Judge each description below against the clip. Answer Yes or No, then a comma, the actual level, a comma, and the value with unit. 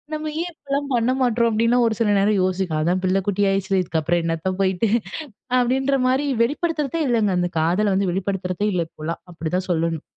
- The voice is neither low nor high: No, high, 200 Hz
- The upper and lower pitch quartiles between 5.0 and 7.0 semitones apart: Yes, wide, 5.6 semitones